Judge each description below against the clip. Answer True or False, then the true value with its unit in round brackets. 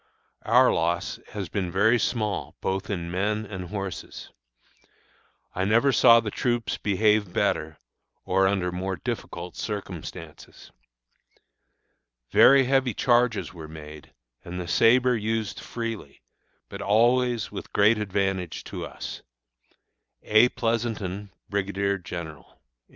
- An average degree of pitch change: True (3.9 semitones)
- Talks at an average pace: False (115 wpm)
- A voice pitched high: False (100 Hz)